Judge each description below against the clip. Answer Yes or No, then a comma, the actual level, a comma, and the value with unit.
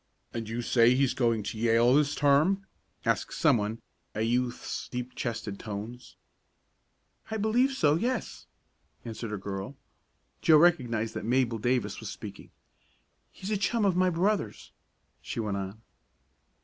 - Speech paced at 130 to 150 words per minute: Yes, average, 140 wpm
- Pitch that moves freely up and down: Yes, wide, 6.7 semitones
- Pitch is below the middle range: Yes, low, 125 Hz